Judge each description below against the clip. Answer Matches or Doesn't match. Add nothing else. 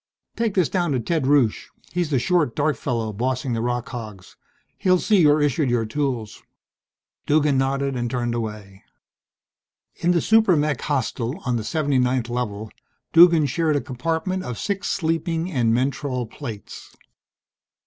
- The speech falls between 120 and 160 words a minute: Matches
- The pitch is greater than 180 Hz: Doesn't match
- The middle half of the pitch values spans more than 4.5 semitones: Matches